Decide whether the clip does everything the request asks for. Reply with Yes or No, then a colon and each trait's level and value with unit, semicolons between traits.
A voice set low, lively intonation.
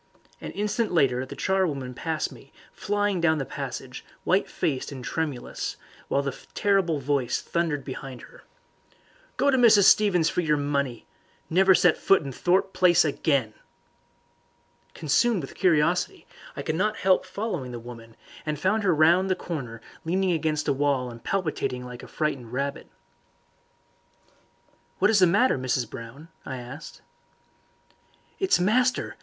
No: medium, 155 Hz; wide, 5.9 semitones